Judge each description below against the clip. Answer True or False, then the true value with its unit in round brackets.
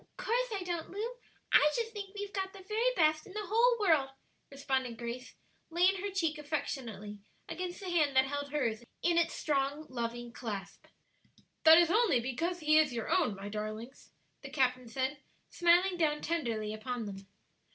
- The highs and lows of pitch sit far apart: True (6.9 semitones)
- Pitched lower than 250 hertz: False (300 Hz)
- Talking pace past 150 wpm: True (170 wpm)